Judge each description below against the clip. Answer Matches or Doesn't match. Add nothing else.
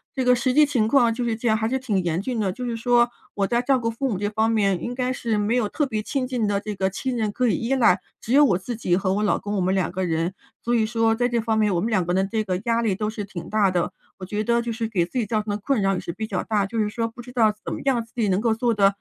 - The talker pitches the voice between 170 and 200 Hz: Doesn't match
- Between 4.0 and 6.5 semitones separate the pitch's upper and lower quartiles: Doesn't match